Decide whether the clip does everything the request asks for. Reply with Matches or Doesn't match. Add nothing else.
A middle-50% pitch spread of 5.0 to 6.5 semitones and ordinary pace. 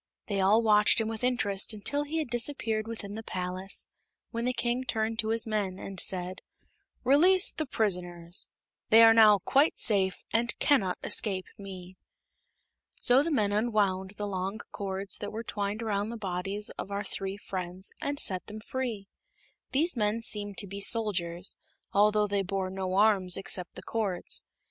Doesn't match